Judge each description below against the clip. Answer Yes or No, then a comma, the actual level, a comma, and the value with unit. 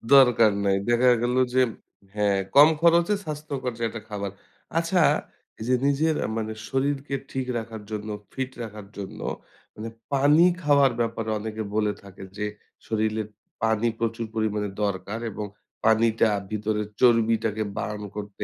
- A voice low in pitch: Yes, low, 115 Hz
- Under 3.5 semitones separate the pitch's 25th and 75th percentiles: No, average, 3.8 semitones